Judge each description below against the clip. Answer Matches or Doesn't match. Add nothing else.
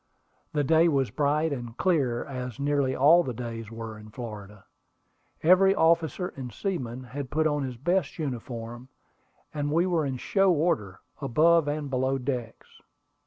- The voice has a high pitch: Doesn't match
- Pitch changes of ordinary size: Matches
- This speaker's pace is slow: Doesn't match